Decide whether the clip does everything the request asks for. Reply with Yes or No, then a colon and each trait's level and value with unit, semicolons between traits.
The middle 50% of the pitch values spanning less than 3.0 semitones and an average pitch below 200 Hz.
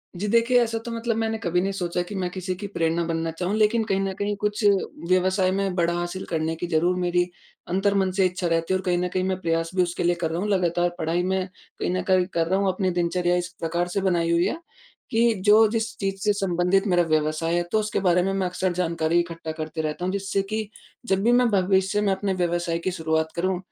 Yes: narrow, 2.4 semitones; medium, 185 Hz